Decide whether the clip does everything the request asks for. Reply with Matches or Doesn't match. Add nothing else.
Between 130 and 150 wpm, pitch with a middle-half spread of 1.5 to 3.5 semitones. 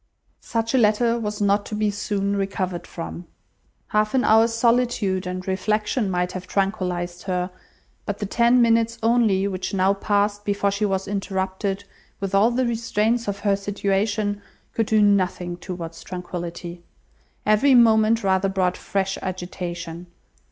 Matches